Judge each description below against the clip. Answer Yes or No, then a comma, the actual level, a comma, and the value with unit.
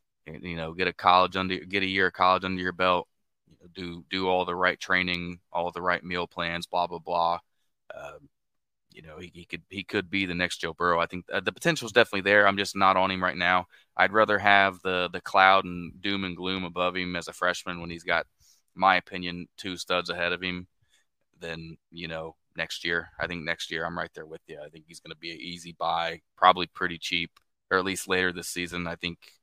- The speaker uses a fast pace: Yes, fast, 240 wpm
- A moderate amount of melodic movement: No, narrow, 1.4 semitones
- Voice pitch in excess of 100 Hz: No, very low, 90 Hz